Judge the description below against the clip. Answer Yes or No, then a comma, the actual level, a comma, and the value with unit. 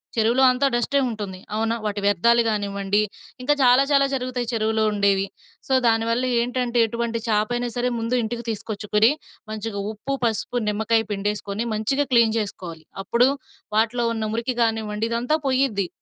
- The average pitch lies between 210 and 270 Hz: Yes, high, 225 Hz